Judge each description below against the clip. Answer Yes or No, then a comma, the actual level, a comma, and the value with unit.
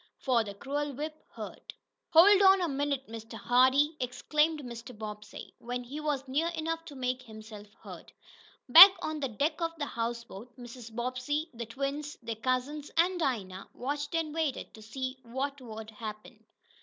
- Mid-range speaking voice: No, very high, 260 Hz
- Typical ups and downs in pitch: Yes, average, 4.4 semitones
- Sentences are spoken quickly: No, average, 165 wpm